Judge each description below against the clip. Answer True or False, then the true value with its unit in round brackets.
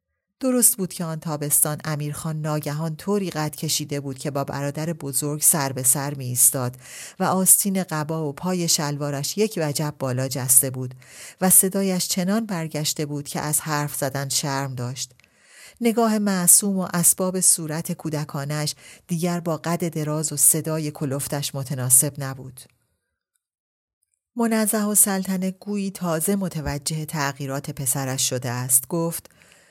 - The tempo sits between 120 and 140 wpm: True (135 wpm)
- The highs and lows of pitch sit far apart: False (4.2 semitones)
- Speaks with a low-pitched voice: False (155 Hz)